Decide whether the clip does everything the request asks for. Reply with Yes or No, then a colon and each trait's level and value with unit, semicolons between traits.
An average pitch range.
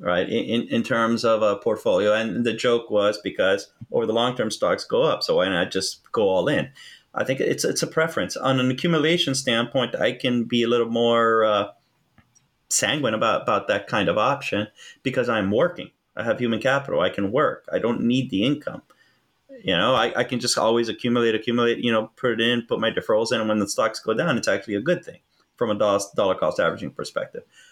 No: wide, 6.0 semitones